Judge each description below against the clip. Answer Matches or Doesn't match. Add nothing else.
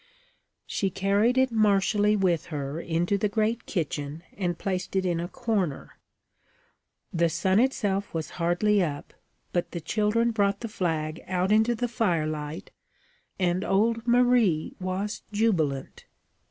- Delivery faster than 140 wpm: Doesn't match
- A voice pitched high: Matches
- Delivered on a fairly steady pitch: Doesn't match